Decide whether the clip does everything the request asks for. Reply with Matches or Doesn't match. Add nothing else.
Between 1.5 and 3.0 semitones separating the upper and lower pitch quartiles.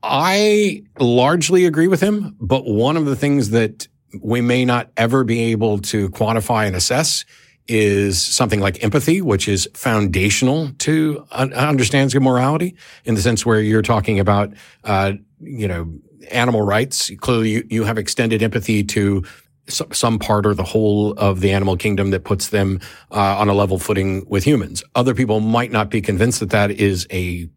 Doesn't match